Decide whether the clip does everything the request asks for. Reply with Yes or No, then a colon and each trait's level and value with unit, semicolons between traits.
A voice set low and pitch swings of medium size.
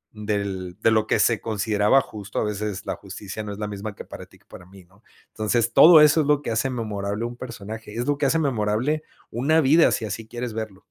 Yes: low, 110 Hz; average, 3.3 semitones